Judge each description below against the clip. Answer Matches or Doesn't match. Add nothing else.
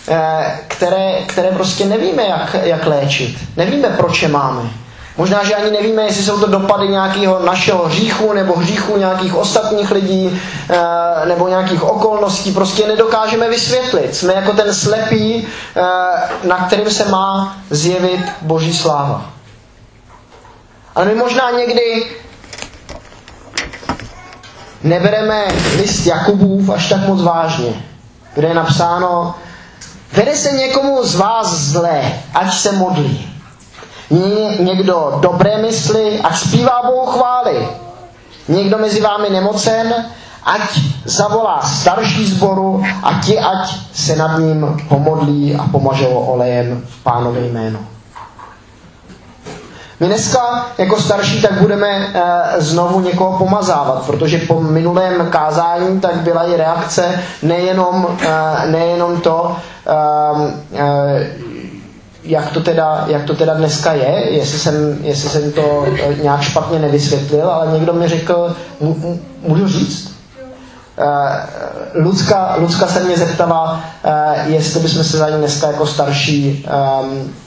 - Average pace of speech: Matches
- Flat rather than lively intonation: Doesn't match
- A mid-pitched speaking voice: Matches